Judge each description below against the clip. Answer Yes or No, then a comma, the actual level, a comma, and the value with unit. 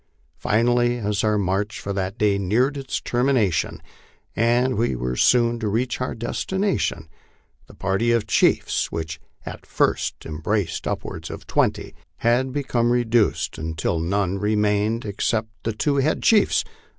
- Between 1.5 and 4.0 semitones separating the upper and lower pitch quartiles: Yes, average, 3.6 semitones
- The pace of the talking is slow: No, average, 145 wpm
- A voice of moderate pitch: No, low, 110 Hz